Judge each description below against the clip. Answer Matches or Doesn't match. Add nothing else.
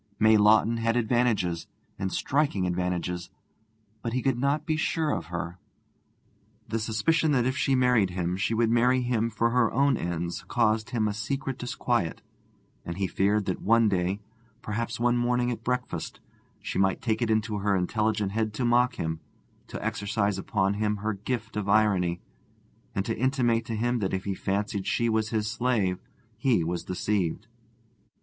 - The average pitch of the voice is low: Matches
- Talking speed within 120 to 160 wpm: Doesn't match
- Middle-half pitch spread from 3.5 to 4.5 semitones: Matches